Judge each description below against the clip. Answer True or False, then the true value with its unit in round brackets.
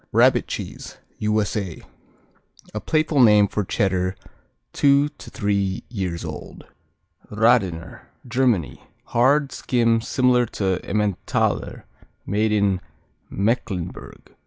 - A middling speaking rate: False (95 wpm)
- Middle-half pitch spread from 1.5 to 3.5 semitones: False (4.2 semitones)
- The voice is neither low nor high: False (105 Hz)